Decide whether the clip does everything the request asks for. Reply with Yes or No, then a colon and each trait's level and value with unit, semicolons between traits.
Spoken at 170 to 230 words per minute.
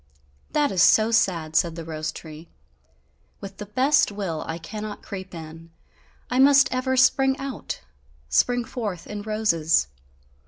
No: average, 145 wpm